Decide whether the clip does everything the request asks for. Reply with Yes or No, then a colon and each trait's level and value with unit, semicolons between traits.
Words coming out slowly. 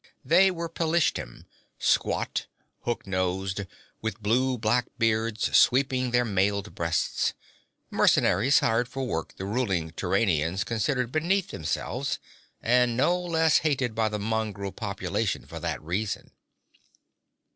Yes: slow, 120 wpm